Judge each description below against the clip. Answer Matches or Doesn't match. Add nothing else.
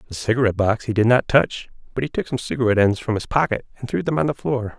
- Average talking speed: Doesn't match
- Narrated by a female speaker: Doesn't match